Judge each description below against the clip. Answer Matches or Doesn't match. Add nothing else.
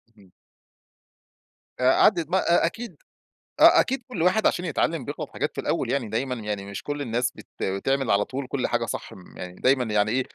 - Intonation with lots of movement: Matches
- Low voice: Matches